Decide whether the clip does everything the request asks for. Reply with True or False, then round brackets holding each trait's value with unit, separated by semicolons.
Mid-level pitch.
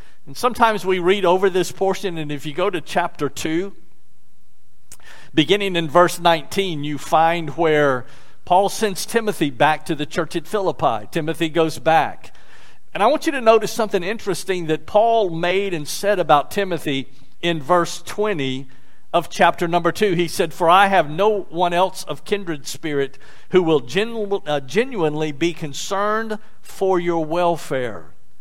True (170 Hz)